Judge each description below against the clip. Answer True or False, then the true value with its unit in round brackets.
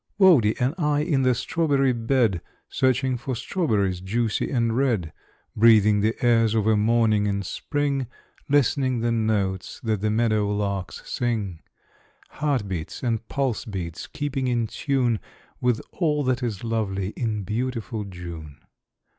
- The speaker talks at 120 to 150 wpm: True (140 wpm)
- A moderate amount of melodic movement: True (4.0 semitones)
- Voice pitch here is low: True (115 Hz)